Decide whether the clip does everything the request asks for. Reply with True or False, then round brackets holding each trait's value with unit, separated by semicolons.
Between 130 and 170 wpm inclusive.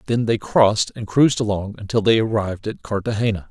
False (190 wpm)